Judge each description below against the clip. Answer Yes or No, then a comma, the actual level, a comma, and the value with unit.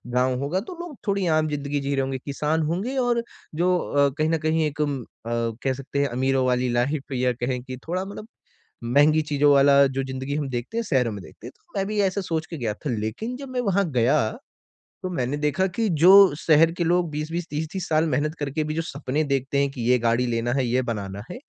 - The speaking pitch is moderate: Yes, medium, 145 Hz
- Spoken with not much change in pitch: No, average, 4.6 semitones